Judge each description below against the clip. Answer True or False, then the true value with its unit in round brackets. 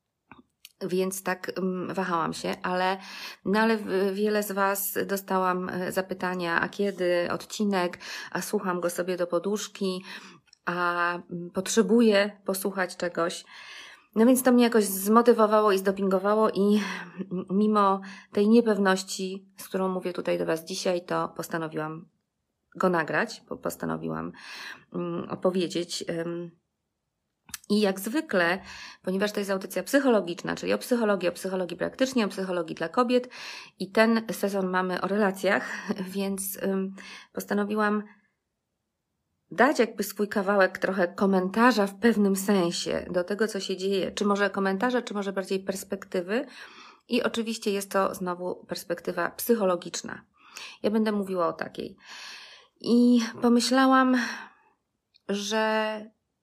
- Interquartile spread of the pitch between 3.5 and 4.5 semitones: False (2.8 semitones)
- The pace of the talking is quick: False (120 wpm)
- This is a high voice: True (195 Hz)